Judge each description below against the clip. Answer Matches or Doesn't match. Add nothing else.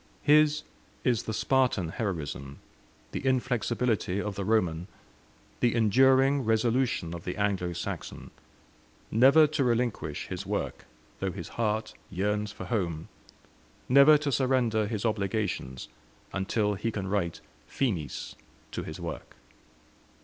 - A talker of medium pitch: Doesn't match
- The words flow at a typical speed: Doesn't match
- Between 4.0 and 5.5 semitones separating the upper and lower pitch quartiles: Matches